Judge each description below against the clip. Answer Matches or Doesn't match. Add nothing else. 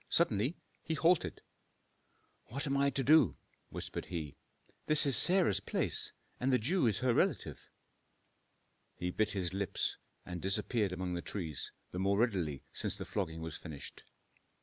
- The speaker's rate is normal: Matches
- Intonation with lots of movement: Matches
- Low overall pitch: Matches